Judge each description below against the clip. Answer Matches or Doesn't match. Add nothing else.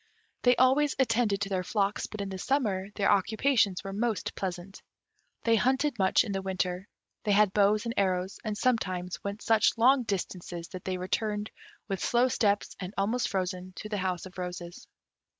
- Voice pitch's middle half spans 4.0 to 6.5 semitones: Doesn't match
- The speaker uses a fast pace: Doesn't match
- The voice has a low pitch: Doesn't match